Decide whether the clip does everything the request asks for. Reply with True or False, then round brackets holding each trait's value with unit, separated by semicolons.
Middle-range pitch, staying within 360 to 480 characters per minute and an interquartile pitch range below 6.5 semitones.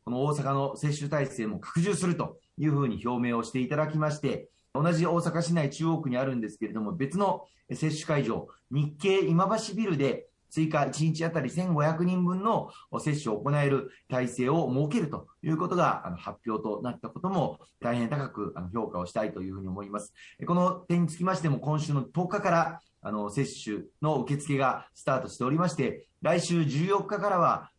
True (150 Hz; 365 characters per minute; 5.4 semitones)